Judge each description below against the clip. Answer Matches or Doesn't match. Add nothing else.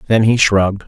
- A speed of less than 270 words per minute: Matches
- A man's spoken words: Matches